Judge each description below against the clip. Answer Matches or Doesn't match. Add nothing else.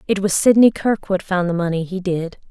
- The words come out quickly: Doesn't match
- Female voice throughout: Matches